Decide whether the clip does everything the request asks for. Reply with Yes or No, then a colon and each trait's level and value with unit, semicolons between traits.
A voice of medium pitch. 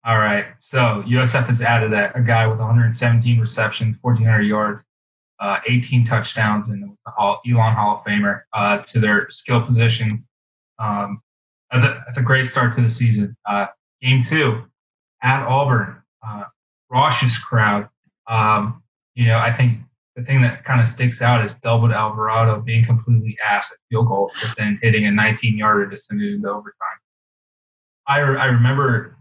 No: low, 115 Hz